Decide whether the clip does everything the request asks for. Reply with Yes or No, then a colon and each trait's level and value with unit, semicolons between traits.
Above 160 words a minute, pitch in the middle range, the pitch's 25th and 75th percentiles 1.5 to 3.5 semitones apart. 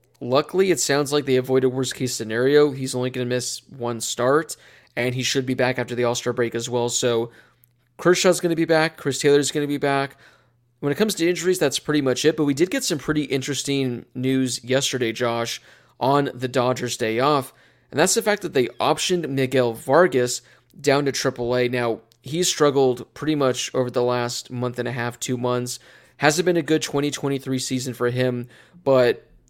No: average, 200 wpm; low, 130 Hz; average, 3.2 semitones